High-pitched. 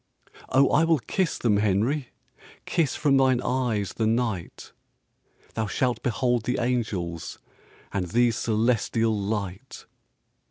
No: low, 115 Hz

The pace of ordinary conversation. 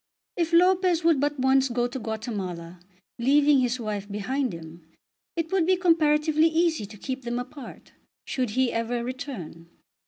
Yes: average, 155 wpm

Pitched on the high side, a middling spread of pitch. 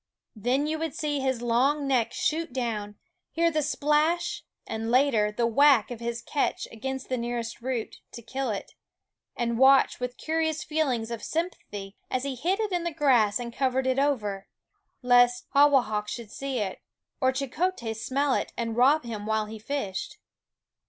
Yes: very high, 255 Hz; average, 4.1 semitones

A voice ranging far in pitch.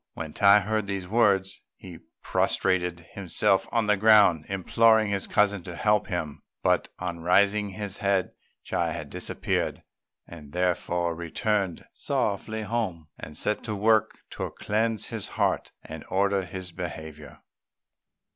No: average, 3.3 semitones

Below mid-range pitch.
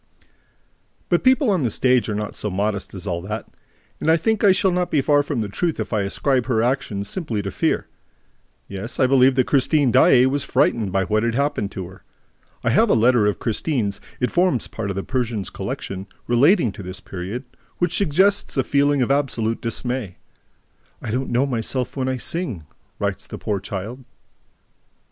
Yes: low, 125 Hz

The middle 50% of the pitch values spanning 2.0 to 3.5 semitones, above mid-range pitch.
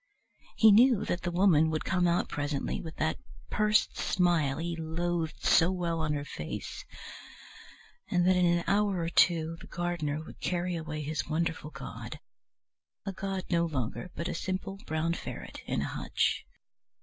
No: narrow, 2.4 semitones; medium, 170 Hz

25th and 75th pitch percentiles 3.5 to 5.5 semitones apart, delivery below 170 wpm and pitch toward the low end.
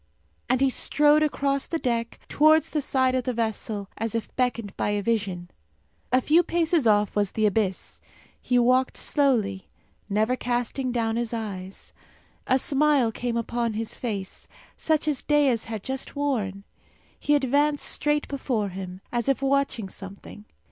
No: average, 4.6 semitones; average, 155 wpm; high, 240 Hz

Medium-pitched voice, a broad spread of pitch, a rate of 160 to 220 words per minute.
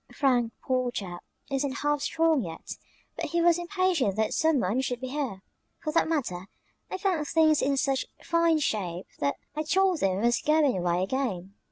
No: very high, 270 Hz; wide, 7.6 semitones; average, 185 wpm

